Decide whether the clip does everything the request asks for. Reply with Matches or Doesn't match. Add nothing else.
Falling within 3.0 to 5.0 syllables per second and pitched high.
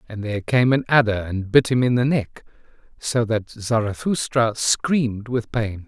Doesn't match